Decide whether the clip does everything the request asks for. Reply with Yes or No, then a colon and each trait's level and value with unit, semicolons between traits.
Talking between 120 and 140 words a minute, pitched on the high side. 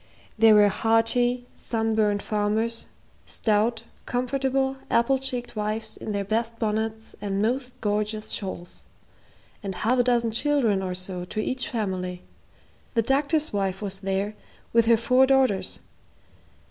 Yes: slow, 135 wpm; high, 225 Hz